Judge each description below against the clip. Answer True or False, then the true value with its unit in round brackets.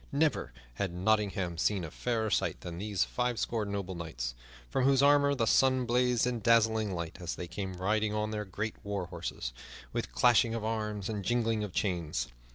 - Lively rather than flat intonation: False (4.2 semitones)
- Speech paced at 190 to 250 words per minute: False (180 wpm)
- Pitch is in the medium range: False (105 Hz)